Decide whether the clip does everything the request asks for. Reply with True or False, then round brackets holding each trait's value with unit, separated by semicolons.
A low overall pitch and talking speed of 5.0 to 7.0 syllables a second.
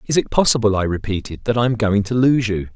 True (110 Hz; 6.1 syllables/s)